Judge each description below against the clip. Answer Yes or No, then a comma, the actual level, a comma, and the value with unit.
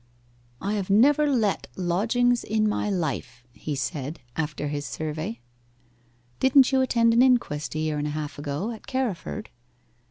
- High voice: Yes, high, 195 Hz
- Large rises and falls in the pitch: Yes, wide, 8.0 semitones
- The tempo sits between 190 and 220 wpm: No, average, 155 wpm